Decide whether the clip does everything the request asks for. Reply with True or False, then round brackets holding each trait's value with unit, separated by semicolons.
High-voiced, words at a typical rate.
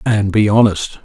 False (105 Hz; 175 wpm)